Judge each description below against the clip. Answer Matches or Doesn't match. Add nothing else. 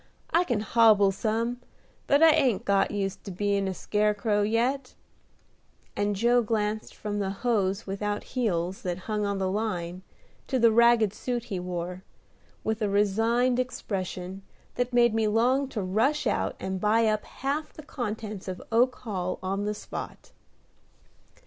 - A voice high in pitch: Matches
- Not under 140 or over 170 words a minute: Matches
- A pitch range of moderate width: Matches